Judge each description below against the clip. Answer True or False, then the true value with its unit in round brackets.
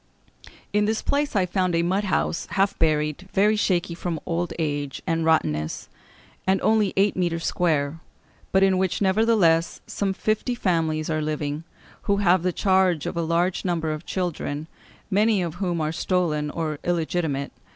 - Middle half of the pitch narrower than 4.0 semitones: True (3.3 semitones)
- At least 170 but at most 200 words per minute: False (160 wpm)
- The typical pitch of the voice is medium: True (175 Hz)